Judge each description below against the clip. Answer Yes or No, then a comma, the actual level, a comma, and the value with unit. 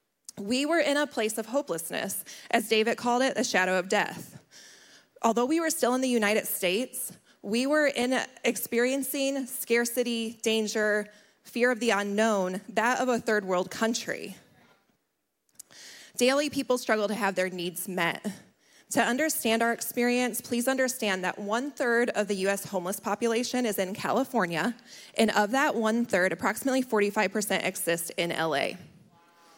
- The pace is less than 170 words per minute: Yes, average, 150 wpm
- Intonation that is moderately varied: Yes, average, 3.7 semitones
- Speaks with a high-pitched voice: Yes, high, 225 Hz